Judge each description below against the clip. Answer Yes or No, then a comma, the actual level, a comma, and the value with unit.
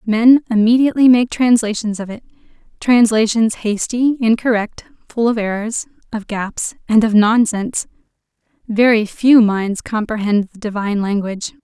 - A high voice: Yes, high, 225 Hz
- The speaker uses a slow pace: Yes, slow, 125 wpm